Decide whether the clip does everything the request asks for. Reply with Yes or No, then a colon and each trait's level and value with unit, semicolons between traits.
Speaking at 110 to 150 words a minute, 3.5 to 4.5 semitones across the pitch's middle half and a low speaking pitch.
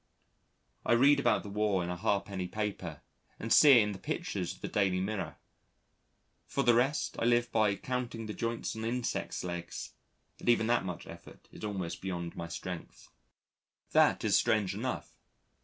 No: average, 175 wpm; average, 4.1 semitones; low, 105 Hz